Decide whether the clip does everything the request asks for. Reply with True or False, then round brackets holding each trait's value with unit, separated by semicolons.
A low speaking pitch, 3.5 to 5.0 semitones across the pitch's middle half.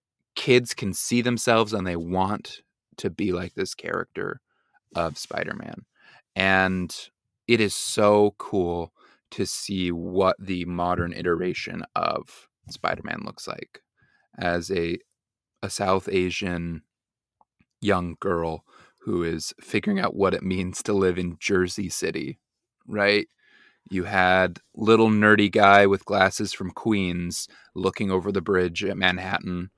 False (95 Hz; 2.7 semitones)